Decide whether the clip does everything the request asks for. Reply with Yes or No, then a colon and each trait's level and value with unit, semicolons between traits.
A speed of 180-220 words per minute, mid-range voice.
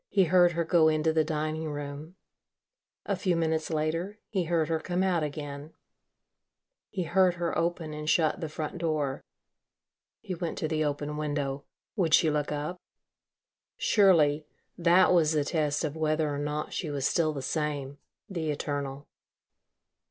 No: average, 160 wpm; medium, 155 Hz